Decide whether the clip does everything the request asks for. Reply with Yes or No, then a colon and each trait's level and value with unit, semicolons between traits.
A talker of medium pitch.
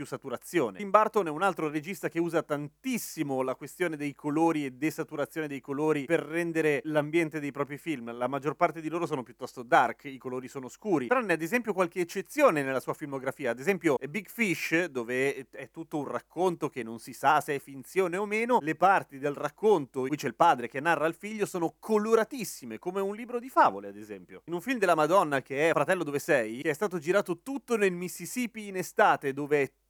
Yes: medium, 155 Hz